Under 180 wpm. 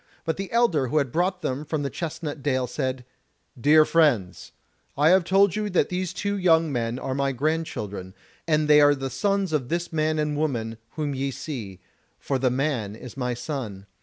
No: average, 190 wpm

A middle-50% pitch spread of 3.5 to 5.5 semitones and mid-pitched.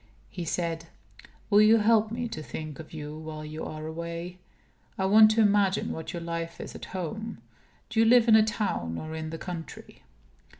Yes: average, 5.2 semitones; medium, 170 Hz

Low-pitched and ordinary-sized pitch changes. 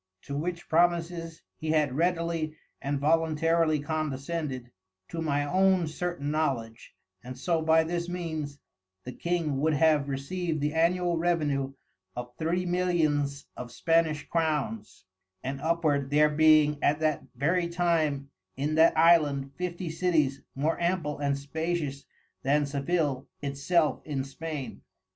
No: medium, 155 Hz; average, 3.0 semitones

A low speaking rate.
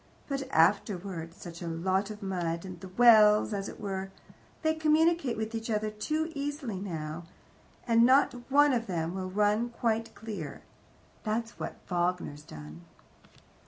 No: average, 150 wpm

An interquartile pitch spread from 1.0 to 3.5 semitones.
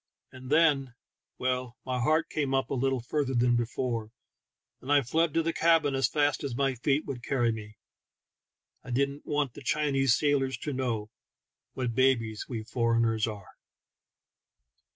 Yes: average, 3.2 semitones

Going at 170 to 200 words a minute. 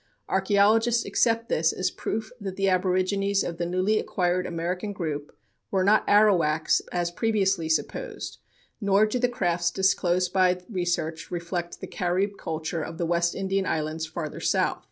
No: average, 155 wpm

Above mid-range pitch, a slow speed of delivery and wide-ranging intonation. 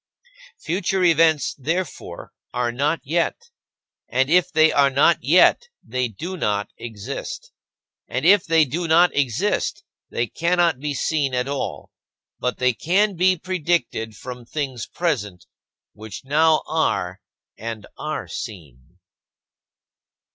No: medium, 145 Hz; slow, 125 wpm; wide, 5.9 semitones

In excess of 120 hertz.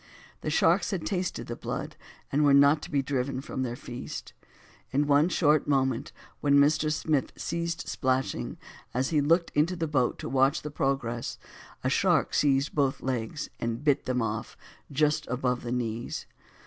Yes: medium, 140 Hz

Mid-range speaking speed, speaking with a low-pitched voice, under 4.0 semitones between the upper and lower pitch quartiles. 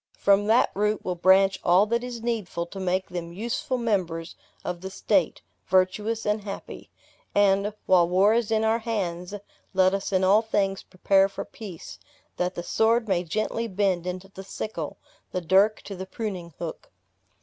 No: average, 170 wpm; high, 195 Hz; average, 2.9 semitones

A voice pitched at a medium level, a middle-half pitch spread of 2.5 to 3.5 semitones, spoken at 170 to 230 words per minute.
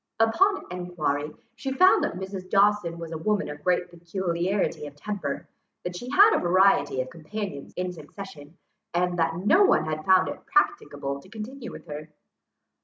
No: medium, 180 Hz; average, 4.8 semitones; average, 175 wpm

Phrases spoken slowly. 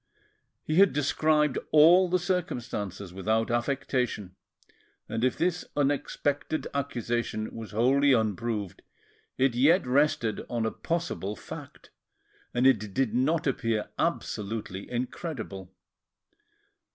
Yes: slow, 105 wpm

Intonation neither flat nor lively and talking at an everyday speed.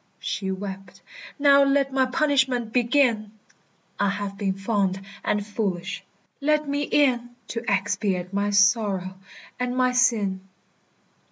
No: average, 4.6 semitones; slow, 120 wpm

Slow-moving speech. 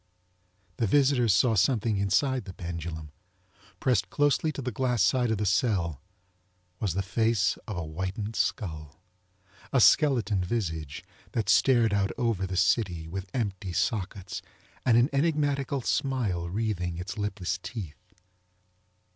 Yes: slow, 130 wpm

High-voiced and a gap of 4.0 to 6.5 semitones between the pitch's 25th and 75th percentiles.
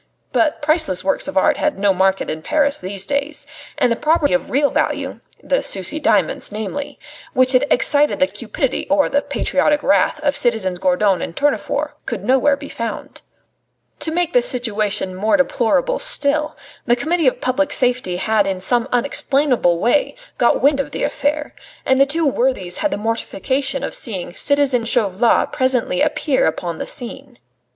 Yes: very high, 260 Hz; wide, 5.4 semitones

